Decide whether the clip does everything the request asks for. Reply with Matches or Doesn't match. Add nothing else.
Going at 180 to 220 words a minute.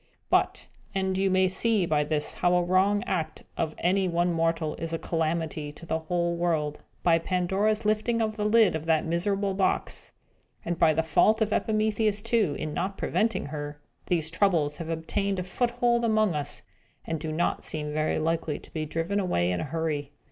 Matches